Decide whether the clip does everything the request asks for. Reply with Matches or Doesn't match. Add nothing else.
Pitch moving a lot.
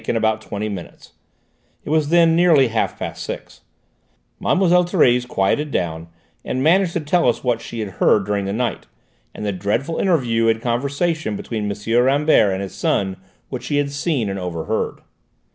Matches